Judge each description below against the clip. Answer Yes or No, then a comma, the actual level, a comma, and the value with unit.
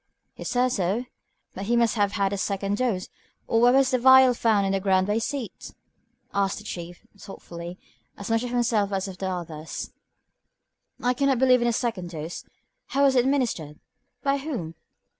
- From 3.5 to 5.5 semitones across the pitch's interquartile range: Yes, average, 4.7 semitones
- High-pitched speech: Yes, high, 215 Hz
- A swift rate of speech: No, average, 190 wpm